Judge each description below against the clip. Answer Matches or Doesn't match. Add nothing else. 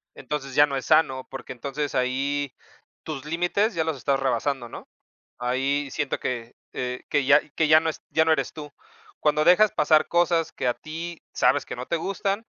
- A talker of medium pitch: Matches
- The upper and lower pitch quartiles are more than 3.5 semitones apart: Doesn't match